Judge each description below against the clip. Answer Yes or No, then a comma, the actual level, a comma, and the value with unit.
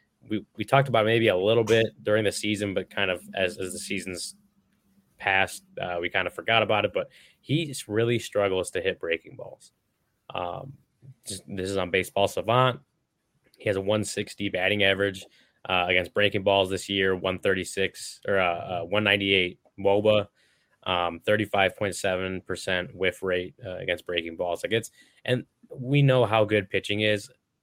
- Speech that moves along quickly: No, average, 160 wpm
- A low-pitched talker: Yes, low, 105 Hz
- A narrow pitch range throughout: No, average, 3.2 semitones